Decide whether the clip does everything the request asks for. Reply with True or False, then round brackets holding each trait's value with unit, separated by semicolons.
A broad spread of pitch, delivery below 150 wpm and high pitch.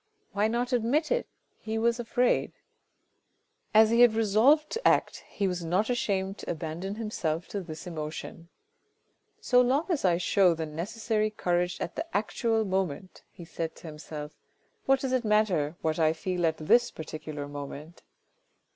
False (6.0 semitones; 165 wpm; 195 Hz)